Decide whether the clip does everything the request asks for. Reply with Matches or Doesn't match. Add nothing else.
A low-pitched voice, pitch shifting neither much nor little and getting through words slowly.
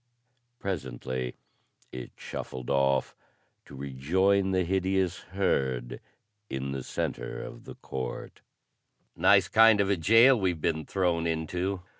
Doesn't match